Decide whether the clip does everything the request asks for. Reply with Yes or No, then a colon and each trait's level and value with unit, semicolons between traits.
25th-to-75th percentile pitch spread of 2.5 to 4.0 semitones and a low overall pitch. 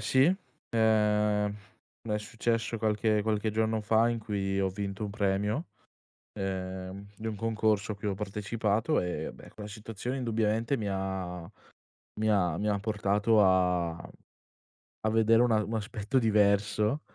No: narrow, 2.0 semitones; low, 105 Hz